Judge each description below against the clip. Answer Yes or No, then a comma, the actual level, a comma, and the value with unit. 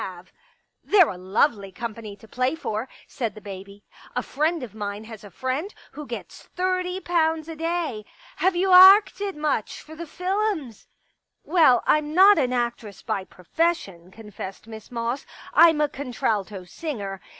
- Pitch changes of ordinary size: No, wide, 8.1 semitones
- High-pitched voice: Yes, very high, 255 Hz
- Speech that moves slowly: No, average, 185 wpm